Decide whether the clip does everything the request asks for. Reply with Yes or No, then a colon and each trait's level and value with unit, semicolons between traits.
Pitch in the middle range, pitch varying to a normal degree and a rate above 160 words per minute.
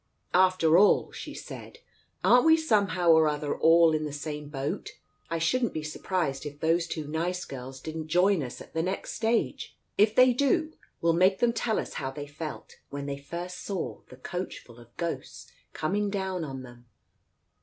Yes: medium, 165 Hz; average, 4.5 semitones; average, 180 wpm